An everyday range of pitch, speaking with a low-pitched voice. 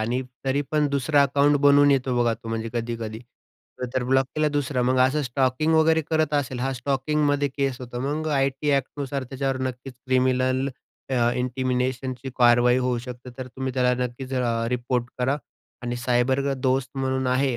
No: narrow, 1.9 semitones; low, 130 Hz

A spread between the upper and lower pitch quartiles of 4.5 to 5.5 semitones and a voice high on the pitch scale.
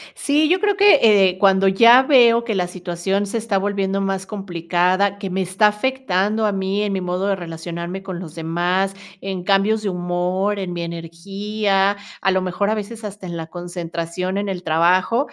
No: average, 2.7 semitones; high, 195 Hz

